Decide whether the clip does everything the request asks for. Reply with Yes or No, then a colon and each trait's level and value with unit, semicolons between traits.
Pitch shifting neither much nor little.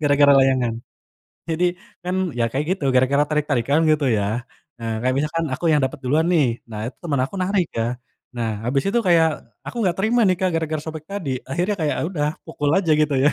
Yes: average, 4.7 semitones